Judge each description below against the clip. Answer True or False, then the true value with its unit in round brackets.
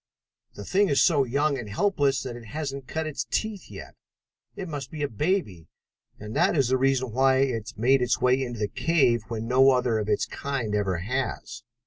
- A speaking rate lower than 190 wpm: False (200 wpm)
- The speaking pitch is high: False (130 Hz)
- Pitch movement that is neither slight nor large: True (3.6 semitones)